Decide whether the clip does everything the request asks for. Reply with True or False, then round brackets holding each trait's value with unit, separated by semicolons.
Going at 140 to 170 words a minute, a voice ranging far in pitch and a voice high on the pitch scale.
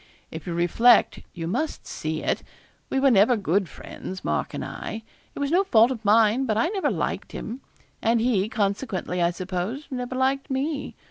False (185 wpm; 5.9 semitones; 225 Hz)